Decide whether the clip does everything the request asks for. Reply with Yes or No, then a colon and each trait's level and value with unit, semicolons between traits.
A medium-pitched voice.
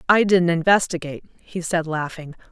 Yes: medium, 170 Hz